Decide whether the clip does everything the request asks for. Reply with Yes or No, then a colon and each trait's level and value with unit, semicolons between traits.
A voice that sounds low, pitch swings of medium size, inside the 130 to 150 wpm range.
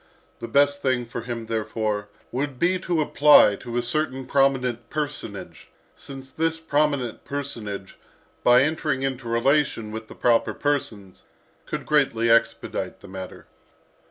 Yes: low, 130 Hz; average, 3.8 semitones; slow, 135 wpm